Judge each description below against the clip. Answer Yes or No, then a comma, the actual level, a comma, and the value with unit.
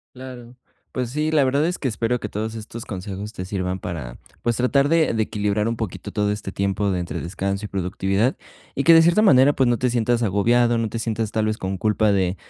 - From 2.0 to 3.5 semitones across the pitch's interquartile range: No, average, 4.0 semitones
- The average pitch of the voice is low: Yes, low, 110 Hz